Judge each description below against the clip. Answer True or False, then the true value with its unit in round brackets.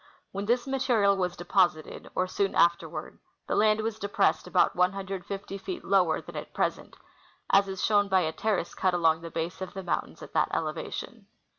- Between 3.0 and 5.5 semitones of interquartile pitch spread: False (2.5 semitones)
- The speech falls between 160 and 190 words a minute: True (180 wpm)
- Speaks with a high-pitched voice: True (195 Hz)